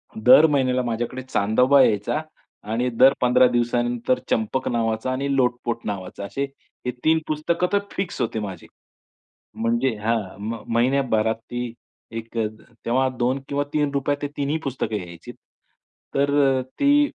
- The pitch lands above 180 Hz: No, low, 125 Hz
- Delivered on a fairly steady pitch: No, average, 3.5 semitones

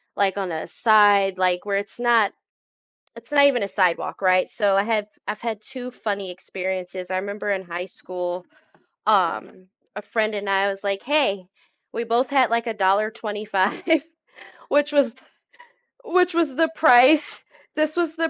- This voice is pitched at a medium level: No, high, 210 Hz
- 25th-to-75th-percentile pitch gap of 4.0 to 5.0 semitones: Yes, average, 4.4 semitones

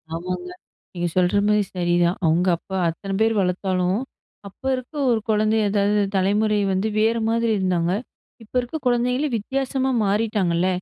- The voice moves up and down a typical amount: Yes, average, 3.8 semitones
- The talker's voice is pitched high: Yes, high, 205 Hz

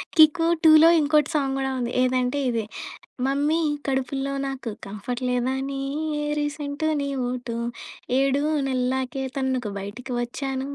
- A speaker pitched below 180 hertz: No, very high, 270 Hz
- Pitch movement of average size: No, narrow, 2.3 semitones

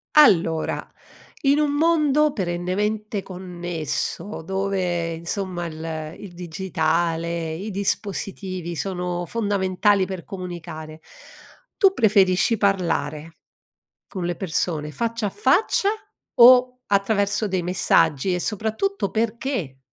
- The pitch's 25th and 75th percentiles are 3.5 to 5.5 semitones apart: Yes, average, 4.0 semitones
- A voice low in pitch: No, medium, 185 Hz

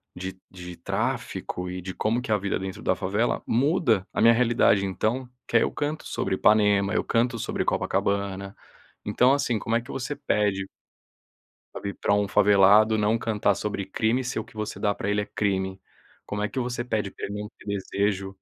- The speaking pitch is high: No, low, 105 Hz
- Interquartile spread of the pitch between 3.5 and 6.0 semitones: No, average, 2.9 semitones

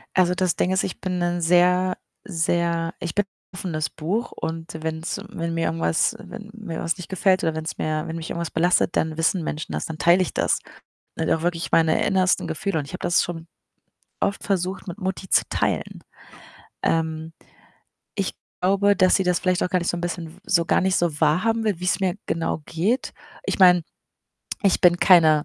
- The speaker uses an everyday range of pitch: No, narrow, 2.2 semitones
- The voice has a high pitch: No, medium, 175 Hz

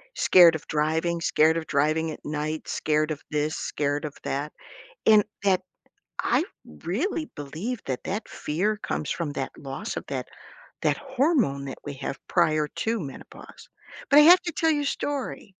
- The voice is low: No, medium, 160 Hz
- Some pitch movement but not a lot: No, wide, 6.5 semitones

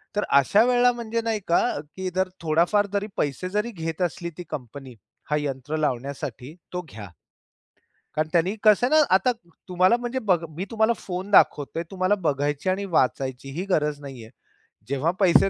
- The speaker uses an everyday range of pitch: No, wide, 6.1 semitones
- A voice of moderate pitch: Yes, medium, 175 Hz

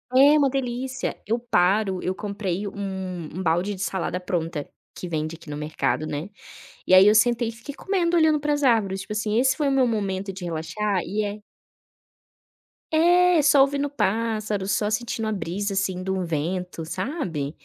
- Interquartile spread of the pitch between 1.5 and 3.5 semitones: No, wide, 5.5 semitones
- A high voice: Yes, high, 205 Hz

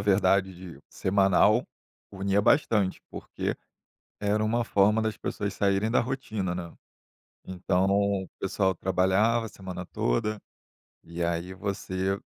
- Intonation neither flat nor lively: No, narrow, 2.3 semitones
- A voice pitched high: No, low, 100 Hz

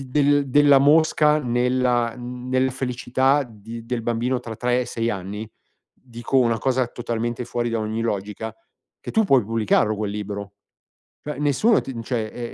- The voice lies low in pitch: Yes, low, 120 Hz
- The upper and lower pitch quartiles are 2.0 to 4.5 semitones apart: Yes, narrow, 2.6 semitones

